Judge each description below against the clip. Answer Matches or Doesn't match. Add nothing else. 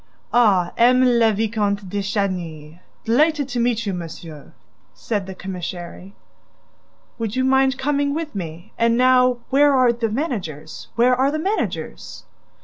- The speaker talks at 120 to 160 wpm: Matches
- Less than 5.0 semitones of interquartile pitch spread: Doesn't match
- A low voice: Doesn't match